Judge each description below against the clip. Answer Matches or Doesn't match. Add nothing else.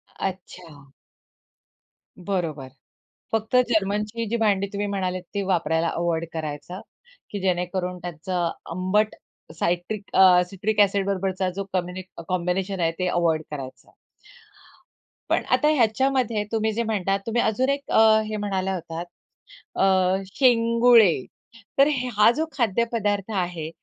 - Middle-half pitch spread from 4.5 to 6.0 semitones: Doesn't match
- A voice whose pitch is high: Matches